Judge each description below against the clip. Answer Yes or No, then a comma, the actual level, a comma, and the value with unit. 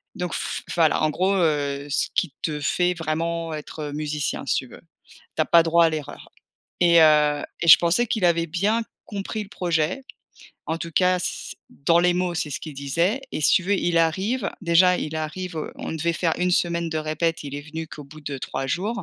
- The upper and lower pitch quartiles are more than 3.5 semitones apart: No, average, 2.7 semitones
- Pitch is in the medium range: Yes, medium, 165 Hz